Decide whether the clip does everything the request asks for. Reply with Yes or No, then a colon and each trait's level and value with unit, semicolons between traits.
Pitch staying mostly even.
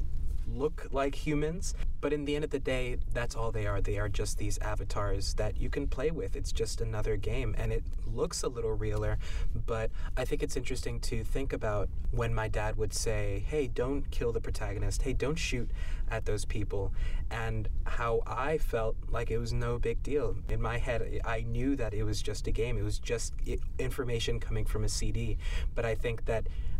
Yes: narrow, 2.2 semitones